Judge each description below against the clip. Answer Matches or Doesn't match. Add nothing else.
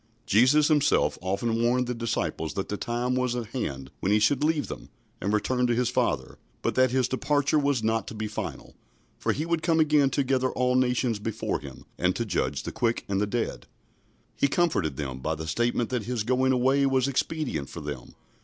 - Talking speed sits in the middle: Doesn't match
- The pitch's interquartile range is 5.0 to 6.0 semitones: Doesn't match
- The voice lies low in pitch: Matches